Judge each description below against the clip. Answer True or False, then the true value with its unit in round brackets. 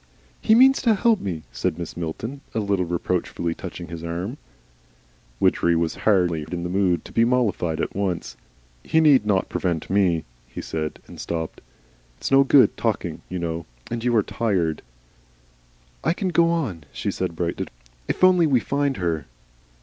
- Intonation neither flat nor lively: False (7.9 semitones)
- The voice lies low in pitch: True (95 Hz)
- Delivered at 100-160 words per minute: False (170 wpm)